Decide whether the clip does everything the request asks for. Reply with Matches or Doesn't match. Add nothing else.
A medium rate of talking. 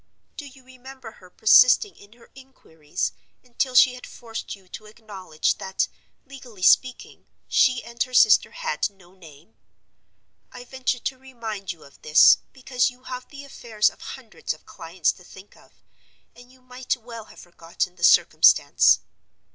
Matches